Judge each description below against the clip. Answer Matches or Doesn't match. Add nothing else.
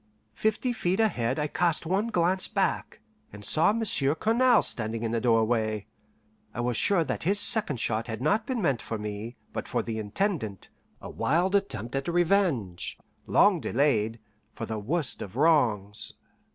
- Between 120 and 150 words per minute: Doesn't match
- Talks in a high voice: Doesn't match